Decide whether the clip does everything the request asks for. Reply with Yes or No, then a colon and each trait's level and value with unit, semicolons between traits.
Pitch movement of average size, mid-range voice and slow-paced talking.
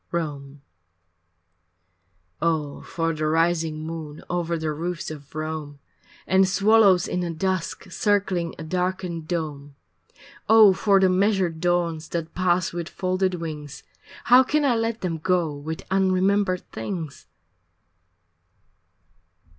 Yes: average, 3.0 semitones; medium, 175 Hz; slow, 125 wpm